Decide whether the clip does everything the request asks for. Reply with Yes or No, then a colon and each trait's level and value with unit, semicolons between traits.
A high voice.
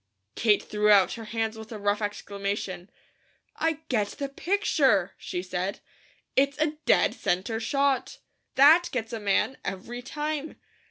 Yes: high, 225 Hz